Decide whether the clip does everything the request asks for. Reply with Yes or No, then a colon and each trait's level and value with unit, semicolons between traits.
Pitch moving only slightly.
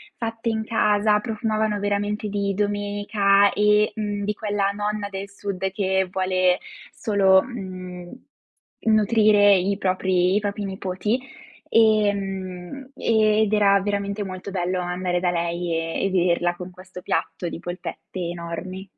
Yes: narrow, 2.2 semitones